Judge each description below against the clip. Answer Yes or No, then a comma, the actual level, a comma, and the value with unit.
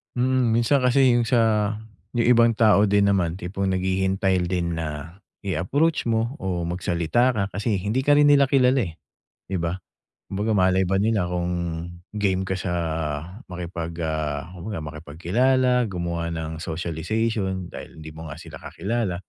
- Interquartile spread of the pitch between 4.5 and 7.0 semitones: Yes, average, 5.0 semitones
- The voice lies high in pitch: No, very low, 95 Hz